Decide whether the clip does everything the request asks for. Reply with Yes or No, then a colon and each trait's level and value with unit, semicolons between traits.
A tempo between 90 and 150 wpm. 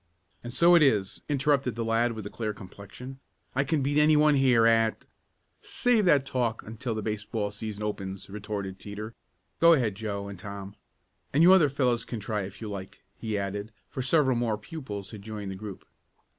No: average, 195 wpm